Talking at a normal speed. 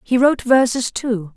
Yes: average, 175 wpm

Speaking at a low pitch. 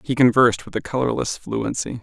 Yes: low, 120 Hz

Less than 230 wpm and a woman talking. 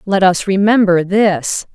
Yes: slow, 135 wpm; female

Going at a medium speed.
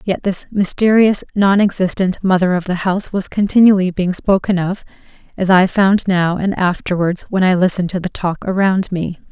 Yes: average, 175 wpm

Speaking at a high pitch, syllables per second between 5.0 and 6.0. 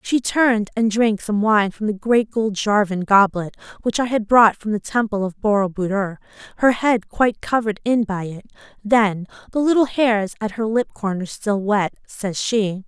No: high, 215 Hz; 4.7 syllables/s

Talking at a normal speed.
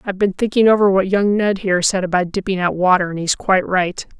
No: fast, 245 wpm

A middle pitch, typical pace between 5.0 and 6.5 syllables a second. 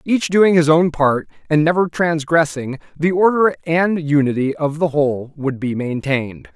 No: medium, 155 Hz; 4.6 syllables/s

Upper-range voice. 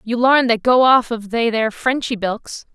Yes: high, 235 Hz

